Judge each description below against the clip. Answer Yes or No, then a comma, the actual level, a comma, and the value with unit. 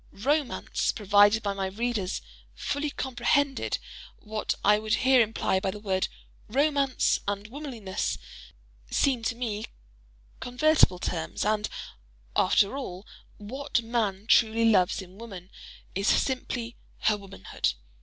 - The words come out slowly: Yes, slow, 115 wpm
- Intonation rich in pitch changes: No, average, 4.1 semitones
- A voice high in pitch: Yes, high, 220 Hz